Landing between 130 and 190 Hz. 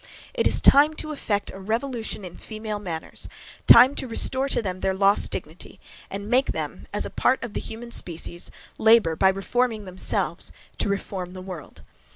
No: high, 210 Hz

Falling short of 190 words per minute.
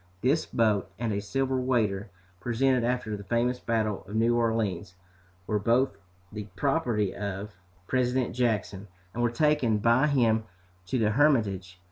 Yes: average, 145 wpm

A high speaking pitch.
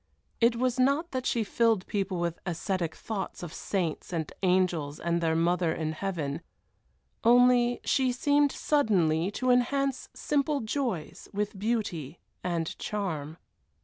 Yes: high, 195 Hz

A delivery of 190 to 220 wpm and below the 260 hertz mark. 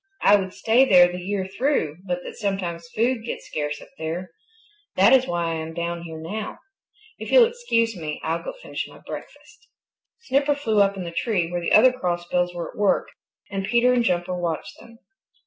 Yes: average, 200 wpm; high, 190 Hz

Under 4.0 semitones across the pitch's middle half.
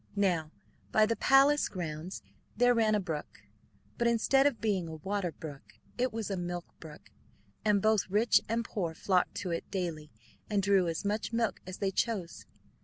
No: average, 4.5 semitones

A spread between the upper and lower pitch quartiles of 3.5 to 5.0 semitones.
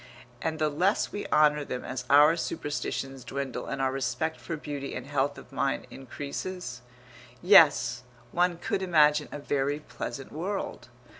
No: average, 3.1 semitones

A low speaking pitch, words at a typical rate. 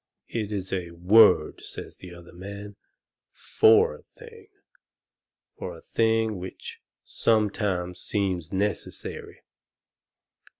No: low, 100 Hz; slow, 100 wpm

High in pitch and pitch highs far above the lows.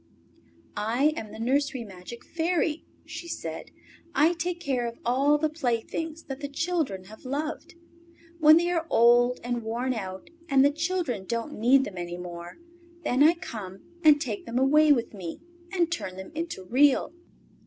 Yes: very high, 265 Hz; wide, 5.7 semitones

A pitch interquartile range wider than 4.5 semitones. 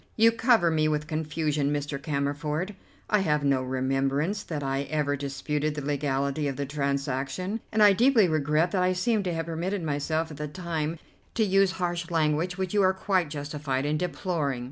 No: average, 4.2 semitones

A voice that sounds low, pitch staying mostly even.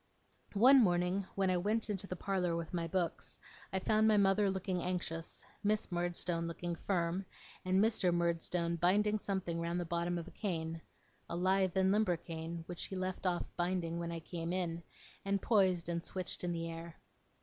No: medium, 180 Hz; narrow, 2.3 semitones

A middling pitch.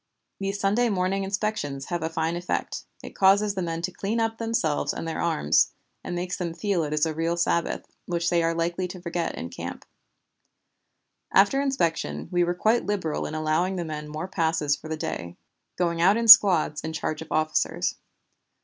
Yes: medium, 170 Hz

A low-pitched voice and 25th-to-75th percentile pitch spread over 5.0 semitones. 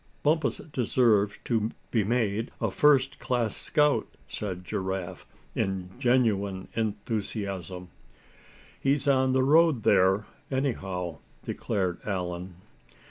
Yes: low, 105 Hz; wide, 5.5 semitones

